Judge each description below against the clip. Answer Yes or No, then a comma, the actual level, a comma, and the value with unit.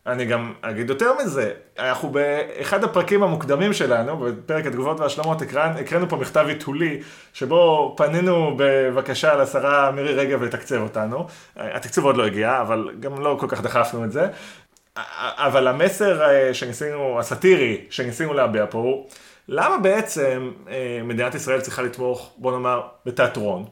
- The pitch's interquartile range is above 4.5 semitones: No, average, 3.8 semitones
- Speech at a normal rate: Yes, average, 135 wpm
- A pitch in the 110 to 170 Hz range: Yes, medium, 140 Hz